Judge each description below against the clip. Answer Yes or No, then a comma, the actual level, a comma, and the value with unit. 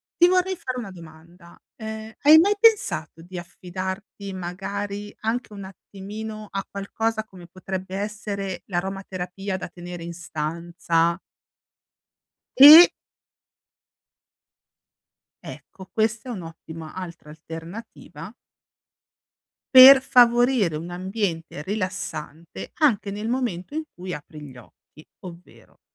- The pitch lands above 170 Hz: Yes, high, 190 Hz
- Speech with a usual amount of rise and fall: Yes, average, 4.2 semitones